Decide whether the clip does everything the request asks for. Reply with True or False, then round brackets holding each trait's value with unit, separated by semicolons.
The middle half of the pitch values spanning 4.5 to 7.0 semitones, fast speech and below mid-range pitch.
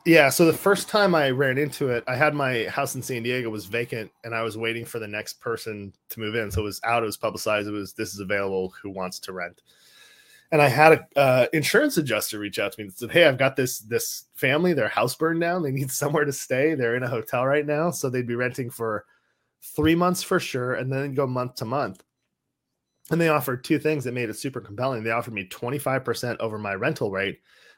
True (4.8 semitones; 240 wpm; 130 Hz)